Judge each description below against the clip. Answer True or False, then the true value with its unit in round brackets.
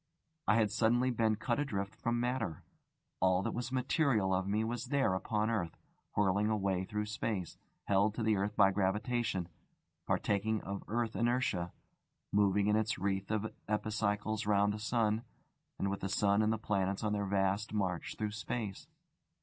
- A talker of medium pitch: False (105 Hz)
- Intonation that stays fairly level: True (2.1 semitones)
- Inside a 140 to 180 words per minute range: True (170 wpm)